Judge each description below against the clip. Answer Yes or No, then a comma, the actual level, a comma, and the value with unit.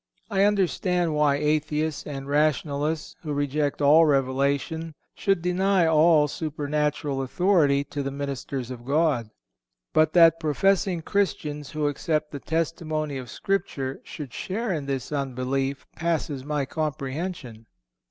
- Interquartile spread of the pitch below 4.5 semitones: Yes, average, 2.9 semitones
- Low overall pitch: No, medium, 150 Hz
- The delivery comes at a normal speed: No, slow, 125 wpm